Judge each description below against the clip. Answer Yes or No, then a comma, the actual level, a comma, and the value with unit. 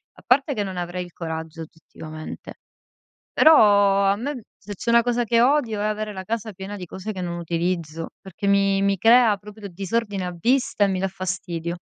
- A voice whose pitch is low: No, high, 195 Hz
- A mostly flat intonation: No, average, 3.6 semitones